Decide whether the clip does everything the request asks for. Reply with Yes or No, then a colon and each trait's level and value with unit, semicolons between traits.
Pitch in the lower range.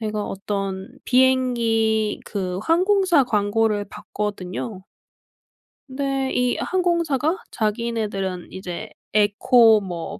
No: high, 220 Hz